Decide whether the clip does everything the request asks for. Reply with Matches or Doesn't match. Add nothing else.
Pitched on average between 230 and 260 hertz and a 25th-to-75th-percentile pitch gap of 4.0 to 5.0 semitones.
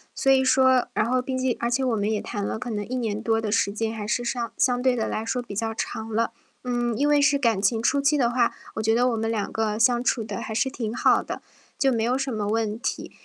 Doesn't match